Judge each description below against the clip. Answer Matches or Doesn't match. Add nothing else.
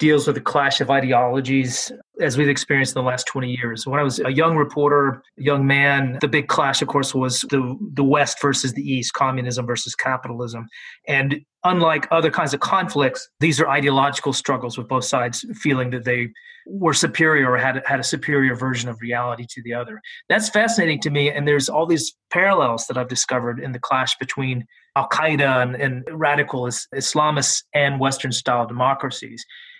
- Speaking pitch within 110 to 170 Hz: Matches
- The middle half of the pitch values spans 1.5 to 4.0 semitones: Matches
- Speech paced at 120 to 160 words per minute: Doesn't match